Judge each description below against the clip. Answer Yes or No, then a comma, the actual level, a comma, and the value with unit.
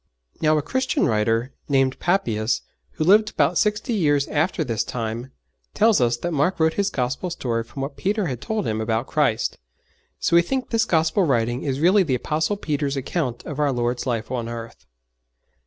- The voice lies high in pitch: No, medium, 140 Hz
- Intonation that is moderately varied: No, wide, 6.6 semitones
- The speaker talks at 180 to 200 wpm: Yes, average, 185 wpm